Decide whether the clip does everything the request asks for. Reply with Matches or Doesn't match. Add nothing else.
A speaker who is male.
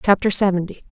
Doesn't match